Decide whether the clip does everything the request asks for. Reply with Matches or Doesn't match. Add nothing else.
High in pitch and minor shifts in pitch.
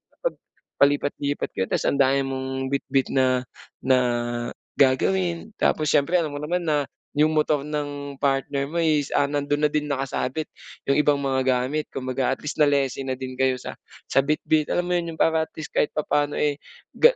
Doesn't match